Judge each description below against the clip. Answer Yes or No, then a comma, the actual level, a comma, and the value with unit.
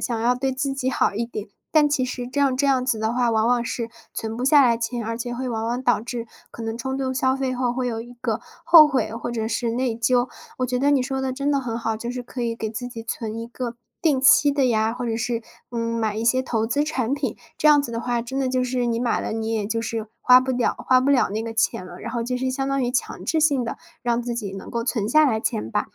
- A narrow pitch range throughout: Yes, narrow, 2.3 semitones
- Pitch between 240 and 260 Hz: Yes, high, 245 Hz